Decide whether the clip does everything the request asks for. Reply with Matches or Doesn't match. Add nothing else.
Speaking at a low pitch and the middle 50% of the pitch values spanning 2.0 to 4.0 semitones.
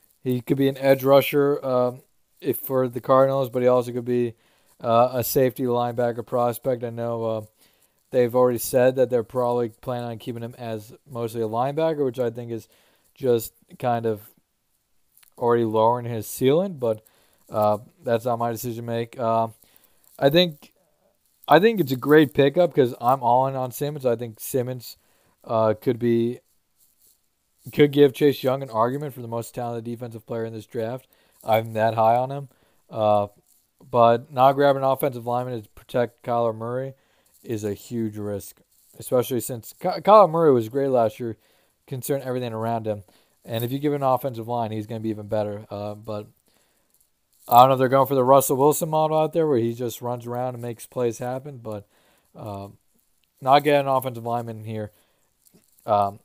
Matches